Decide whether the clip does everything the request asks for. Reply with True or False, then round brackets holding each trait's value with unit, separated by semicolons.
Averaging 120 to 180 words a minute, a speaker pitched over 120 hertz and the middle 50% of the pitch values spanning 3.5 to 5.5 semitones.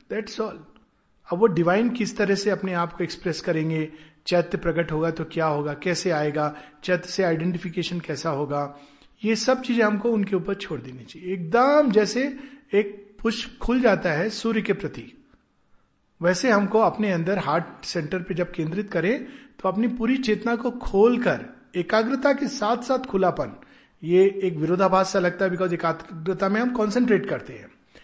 True (170 wpm; 190 Hz; 4.7 semitones)